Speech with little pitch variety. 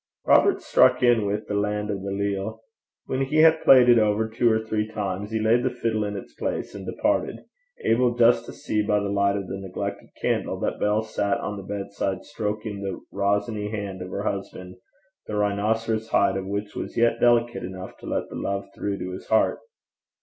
Yes: narrow, 2.1 semitones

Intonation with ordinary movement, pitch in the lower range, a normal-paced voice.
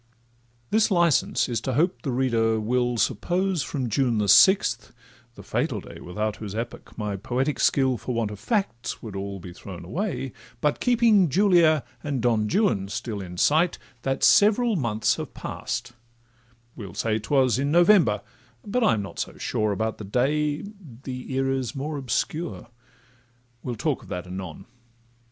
No: wide, 6.7 semitones; low, 125 Hz; average, 160 wpm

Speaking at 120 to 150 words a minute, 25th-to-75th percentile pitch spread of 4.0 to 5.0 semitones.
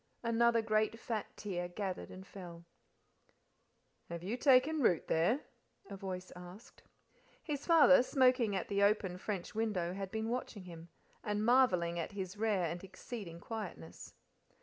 Yes: average, 145 wpm; average, 4.4 semitones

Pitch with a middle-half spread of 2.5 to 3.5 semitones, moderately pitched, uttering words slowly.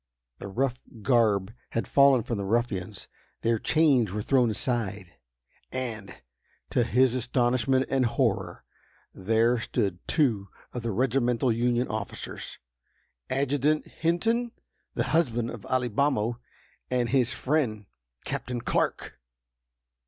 No: average, 3.0 semitones; low, 120 Hz; slow, 115 wpm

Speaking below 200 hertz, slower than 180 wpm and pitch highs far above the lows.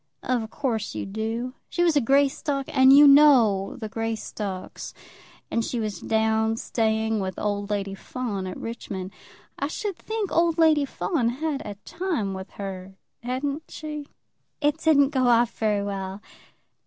No: high, 230 Hz; average, 155 wpm; wide, 5.7 semitones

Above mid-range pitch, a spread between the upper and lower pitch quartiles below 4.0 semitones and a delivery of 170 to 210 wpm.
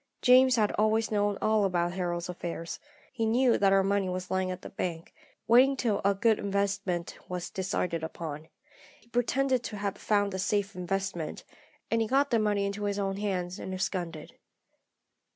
Yes: high, 200 Hz; average, 3.0 semitones; average, 175 wpm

